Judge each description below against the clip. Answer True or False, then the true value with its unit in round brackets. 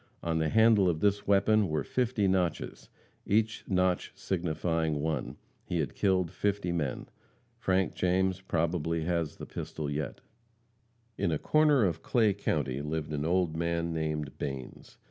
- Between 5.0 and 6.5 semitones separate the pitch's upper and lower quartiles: False (3.7 semitones)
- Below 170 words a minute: True (145 wpm)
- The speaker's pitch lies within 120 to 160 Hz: False (85 Hz)